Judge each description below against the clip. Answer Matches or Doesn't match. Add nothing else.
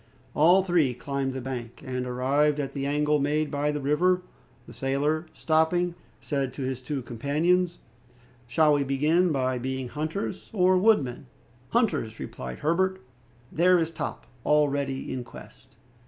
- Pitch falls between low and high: Matches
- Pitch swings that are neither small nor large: Matches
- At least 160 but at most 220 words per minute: Doesn't match